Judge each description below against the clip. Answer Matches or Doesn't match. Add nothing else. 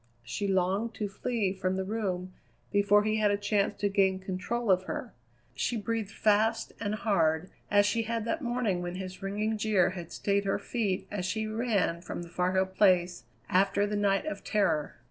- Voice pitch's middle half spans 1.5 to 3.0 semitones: Matches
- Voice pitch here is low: Doesn't match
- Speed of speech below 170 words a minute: Doesn't match